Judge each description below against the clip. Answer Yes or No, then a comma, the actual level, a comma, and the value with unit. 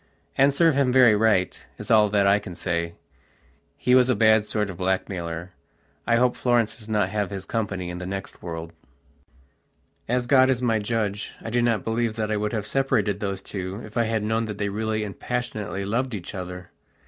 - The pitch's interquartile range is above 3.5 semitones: No, average, 3.2 semitones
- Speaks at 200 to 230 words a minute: Yes, fast, 205 wpm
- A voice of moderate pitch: No, low, 105 Hz